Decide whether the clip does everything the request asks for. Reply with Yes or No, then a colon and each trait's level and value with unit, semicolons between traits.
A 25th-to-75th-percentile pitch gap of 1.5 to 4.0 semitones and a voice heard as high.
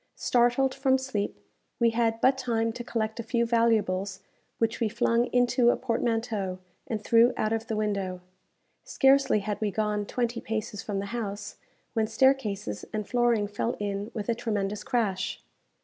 Yes: narrow, 2.6 semitones; high, 225 Hz